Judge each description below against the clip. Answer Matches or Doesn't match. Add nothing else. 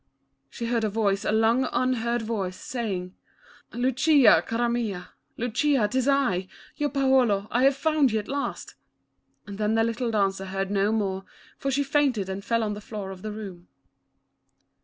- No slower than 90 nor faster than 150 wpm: Doesn't match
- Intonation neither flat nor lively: Matches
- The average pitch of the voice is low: Doesn't match